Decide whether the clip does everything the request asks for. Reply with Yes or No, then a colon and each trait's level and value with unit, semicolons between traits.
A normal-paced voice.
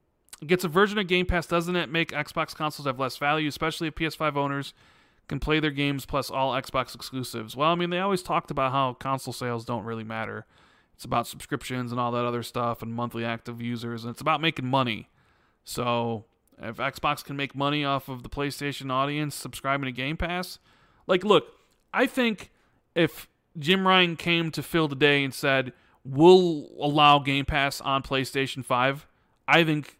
Yes: average, 190 wpm